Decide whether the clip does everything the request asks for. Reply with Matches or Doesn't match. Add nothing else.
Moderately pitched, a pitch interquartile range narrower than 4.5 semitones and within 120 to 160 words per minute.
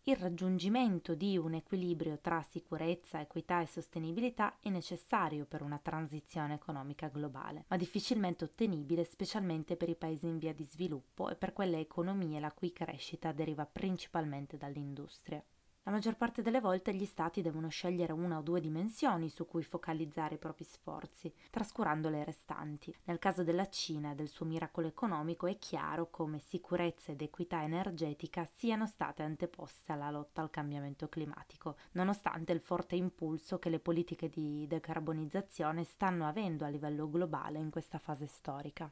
Matches